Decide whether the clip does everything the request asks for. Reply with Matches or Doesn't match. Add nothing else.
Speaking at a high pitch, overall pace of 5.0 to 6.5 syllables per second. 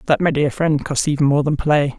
Doesn't match